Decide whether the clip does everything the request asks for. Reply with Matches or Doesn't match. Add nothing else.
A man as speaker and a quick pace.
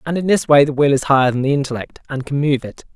Matches